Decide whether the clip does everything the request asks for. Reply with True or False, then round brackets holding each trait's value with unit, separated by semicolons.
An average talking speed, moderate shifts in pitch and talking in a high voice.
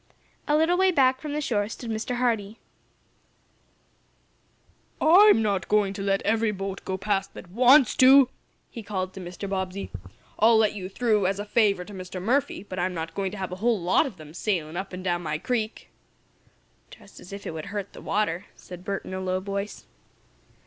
True (195 wpm; 3.5 semitones; 200 Hz)